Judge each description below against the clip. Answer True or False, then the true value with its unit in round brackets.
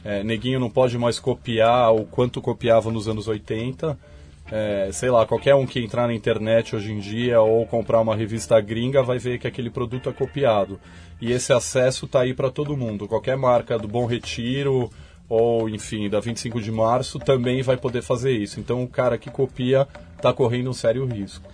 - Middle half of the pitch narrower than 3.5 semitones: True (2.5 semitones)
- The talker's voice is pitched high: False (120 Hz)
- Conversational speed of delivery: False (195 wpm)